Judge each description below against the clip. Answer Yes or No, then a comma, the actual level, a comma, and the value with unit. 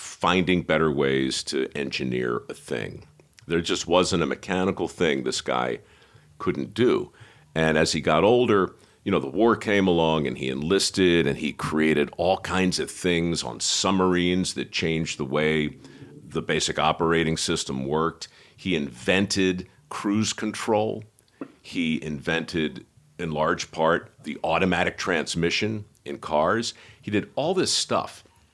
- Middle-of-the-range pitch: No, very low, 85 Hz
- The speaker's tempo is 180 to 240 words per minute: No, average, 145 wpm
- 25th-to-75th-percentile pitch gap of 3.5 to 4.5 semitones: Yes, average, 4.0 semitones